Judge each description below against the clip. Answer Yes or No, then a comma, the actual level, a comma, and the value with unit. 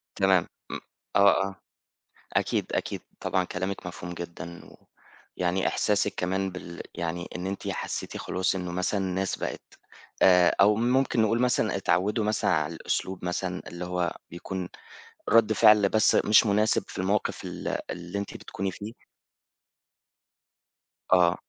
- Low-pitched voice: Yes, very low, 95 Hz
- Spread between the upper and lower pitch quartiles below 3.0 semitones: Yes, narrow, 2.6 semitones